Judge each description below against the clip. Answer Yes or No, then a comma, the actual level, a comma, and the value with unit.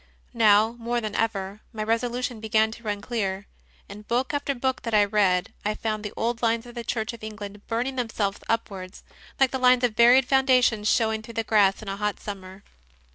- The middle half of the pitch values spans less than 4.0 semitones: Yes, narrow, 2.5 semitones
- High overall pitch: Yes, high, 220 Hz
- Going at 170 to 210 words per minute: Yes, fast, 205 wpm